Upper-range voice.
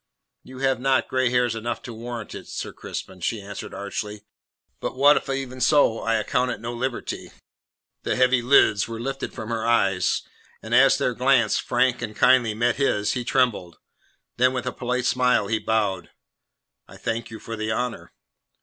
No: low, 120 Hz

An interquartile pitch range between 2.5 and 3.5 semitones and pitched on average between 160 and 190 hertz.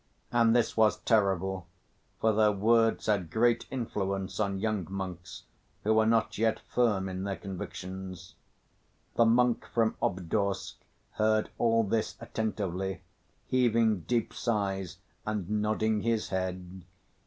No: average, 2.9 semitones; low, 105 Hz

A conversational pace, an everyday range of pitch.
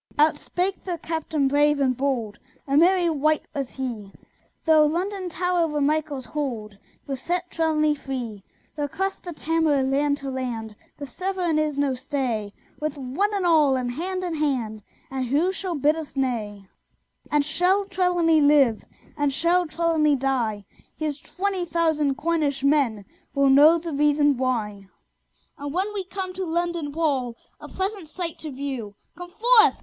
Yes: average, 160 wpm; average, 4.2 semitones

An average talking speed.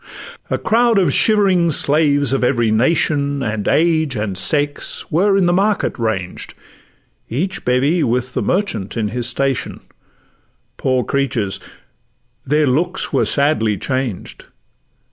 No: slow, 130 wpm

